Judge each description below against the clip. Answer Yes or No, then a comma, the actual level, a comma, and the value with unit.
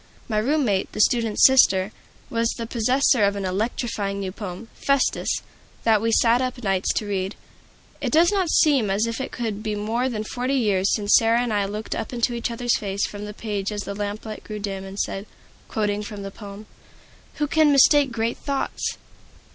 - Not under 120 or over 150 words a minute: No, average, 195 wpm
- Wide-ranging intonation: No, average, 3.2 semitones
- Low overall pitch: No, high, 220 Hz